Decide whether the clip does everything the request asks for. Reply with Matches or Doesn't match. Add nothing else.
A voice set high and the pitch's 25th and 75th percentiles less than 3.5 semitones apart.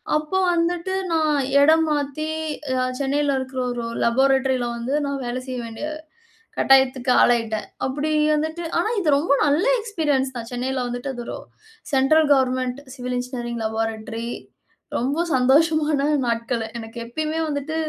Doesn't match